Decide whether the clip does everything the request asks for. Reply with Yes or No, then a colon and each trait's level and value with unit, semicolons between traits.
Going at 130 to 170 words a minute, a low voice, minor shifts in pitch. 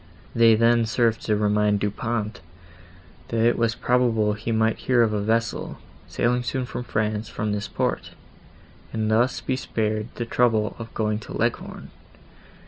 Yes: average, 160 wpm; low, 110 Hz; narrow, 1.7 semitones